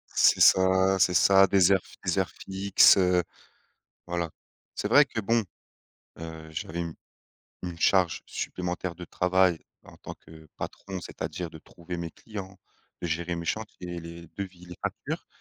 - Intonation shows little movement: Yes, narrow, 2.2 semitones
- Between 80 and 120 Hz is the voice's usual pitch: Yes, very low, 90 Hz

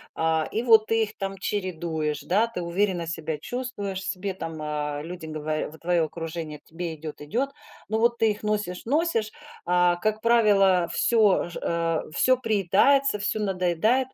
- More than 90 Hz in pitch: Yes, high, 190 Hz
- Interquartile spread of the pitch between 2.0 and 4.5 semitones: No, average, 4.9 semitones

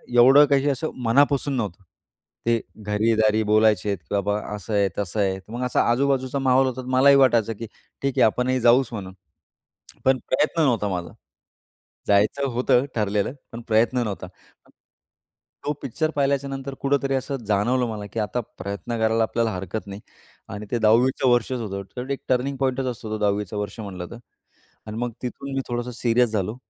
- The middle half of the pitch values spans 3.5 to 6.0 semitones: Yes, average, 4.0 semitones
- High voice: No, low, 120 Hz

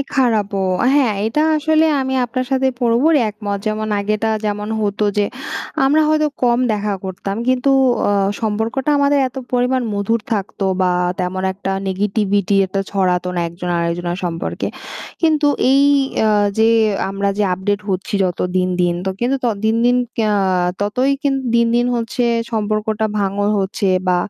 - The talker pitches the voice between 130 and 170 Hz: No, high, 215 Hz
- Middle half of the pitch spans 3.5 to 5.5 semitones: Yes, average, 4.1 semitones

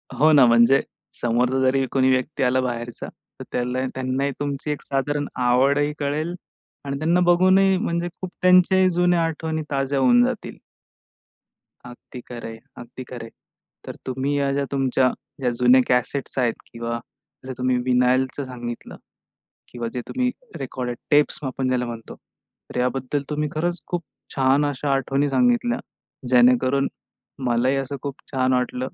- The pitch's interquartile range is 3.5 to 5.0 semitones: No, average, 2.8 semitones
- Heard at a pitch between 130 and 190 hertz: Yes, low, 135 Hz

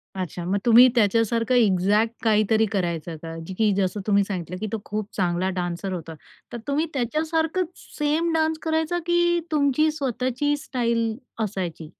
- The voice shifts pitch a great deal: Yes, wide, 7.5 semitones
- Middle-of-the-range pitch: No, high, 225 Hz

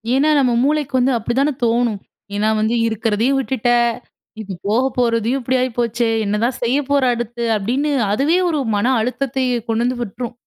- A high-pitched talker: Yes, high, 240 Hz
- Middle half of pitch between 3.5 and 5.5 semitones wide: No, average, 2.8 semitones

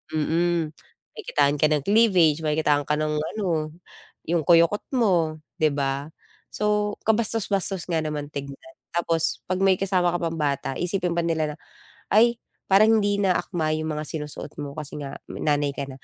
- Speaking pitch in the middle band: Yes, medium, 165 Hz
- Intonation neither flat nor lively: Yes, average, 4.1 semitones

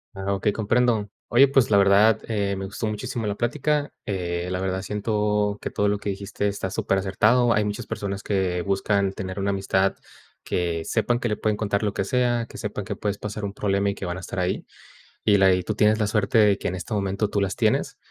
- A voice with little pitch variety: Yes, narrow, 1.8 semitones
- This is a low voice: Yes, low, 100 Hz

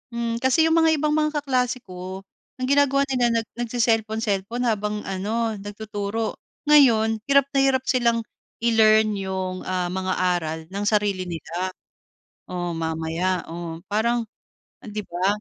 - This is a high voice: Yes, high, 215 Hz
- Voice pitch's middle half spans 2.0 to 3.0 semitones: No, average, 4.5 semitones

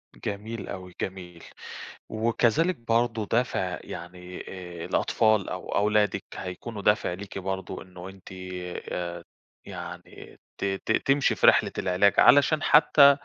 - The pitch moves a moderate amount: Yes, average, 4.1 semitones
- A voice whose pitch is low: Yes, low, 100 Hz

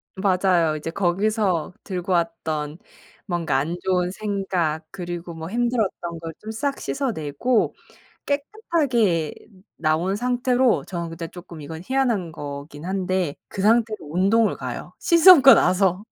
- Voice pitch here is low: No, medium, 185 Hz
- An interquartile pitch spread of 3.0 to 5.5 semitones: Yes, average, 5.2 semitones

